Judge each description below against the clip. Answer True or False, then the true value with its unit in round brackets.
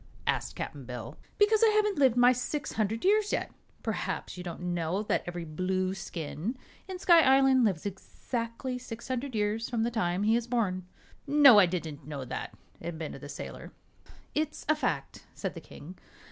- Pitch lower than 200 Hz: False (220 Hz)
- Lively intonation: True (7.0 semitones)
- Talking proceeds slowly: False (175 wpm)